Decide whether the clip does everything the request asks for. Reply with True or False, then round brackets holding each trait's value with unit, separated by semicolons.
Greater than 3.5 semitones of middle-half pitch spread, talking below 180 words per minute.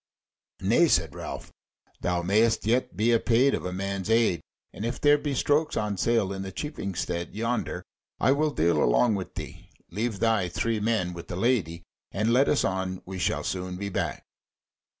False (4.4 semitones; 185 wpm)